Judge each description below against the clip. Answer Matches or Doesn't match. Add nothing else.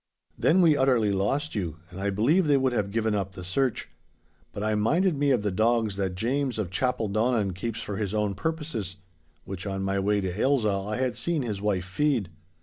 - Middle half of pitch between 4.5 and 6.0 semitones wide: Matches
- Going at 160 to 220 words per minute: Matches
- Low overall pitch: Matches